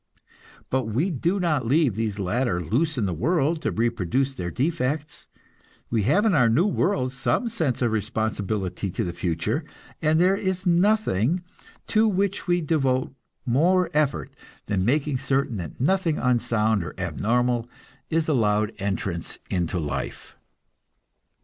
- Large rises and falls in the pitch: Yes, wide, 7.4 semitones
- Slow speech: No, average, 145 wpm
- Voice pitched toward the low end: Yes, low, 130 Hz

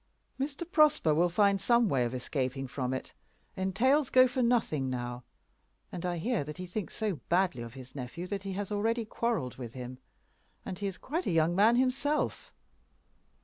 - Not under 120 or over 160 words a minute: No, average, 185 wpm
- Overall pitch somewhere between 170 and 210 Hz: Yes, high, 190 Hz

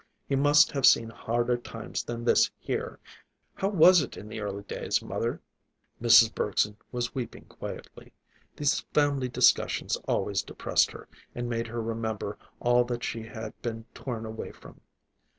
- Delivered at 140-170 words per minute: Yes, average, 155 wpm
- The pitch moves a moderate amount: No, narrow, 2.1 semitones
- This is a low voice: Yes, low, 120 Hz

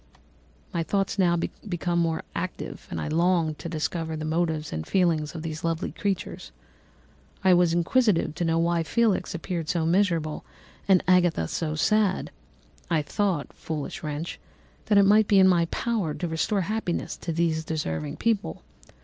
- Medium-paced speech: Yes, average, 160 wpm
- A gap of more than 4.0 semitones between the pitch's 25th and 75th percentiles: No, average, 2.9 semitones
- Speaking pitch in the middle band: Yes, medium, 170 Hz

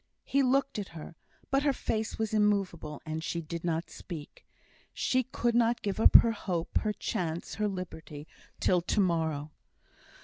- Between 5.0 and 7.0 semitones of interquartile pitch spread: Yes, wide, 5.6 semitones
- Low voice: No, high, 190 Hz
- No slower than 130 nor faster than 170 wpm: Yes, average, 165 wpm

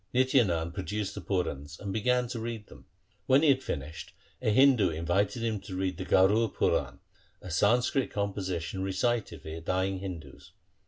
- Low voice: Yes, very low, 95 Hz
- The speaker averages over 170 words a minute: No, average, 165 wpm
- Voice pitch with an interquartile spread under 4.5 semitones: No, average, 4.8 semitones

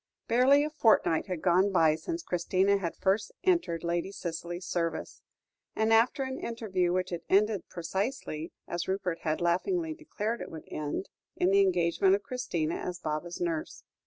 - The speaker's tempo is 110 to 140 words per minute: No, average, 160 wpm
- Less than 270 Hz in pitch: Yes, medium, 185 Hz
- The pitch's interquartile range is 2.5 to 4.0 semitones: No, average, 4.6 semitones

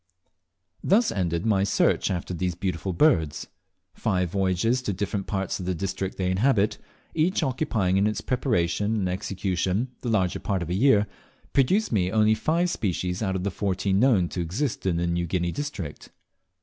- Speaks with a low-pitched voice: Yes, very low, 95 Hz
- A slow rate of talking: No, average, 175 wpm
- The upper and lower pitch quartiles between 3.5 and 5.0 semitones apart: Yes, average, 3.8 semitones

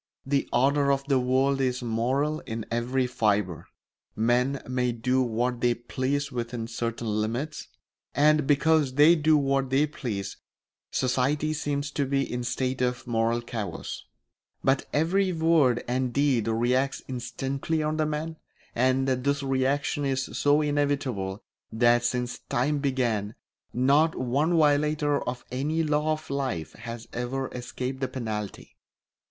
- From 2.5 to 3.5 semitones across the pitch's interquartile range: Yes, average, 3.1 semitones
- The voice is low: Yes, low, 130 Hz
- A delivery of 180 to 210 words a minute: No, average, 140 wpm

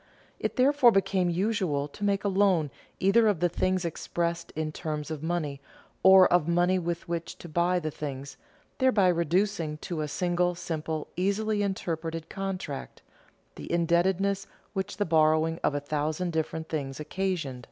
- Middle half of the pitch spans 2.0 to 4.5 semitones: Yes, average, 3.5 semitones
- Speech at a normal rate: Yes, average, 155 wpm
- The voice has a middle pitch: Yes, medium, 175 Hz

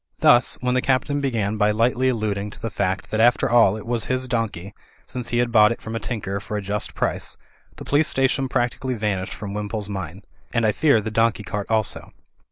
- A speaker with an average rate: No, fast, 220 wpm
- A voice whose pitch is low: Yes, low, 110 Hz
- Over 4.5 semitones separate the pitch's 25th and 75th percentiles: No, average, 2.9 semitones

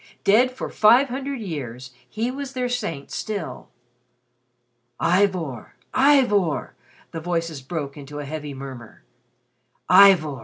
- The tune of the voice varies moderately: No, wide, 8.9 semitones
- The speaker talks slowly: Yes, slow, 115 wpm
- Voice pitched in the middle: Yes, medium, 175 Hz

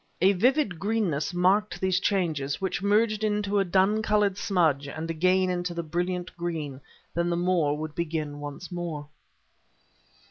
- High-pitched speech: No, medium, 180 Hz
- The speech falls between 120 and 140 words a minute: No, average, 150 wpm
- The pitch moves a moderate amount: Yes, average, 3.8 semitones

